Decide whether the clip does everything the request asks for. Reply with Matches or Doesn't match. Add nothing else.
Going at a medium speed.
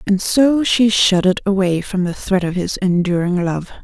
Matches